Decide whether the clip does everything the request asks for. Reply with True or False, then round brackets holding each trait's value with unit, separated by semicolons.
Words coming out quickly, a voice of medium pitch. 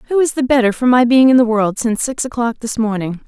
False (275 wpm; 240 Hz)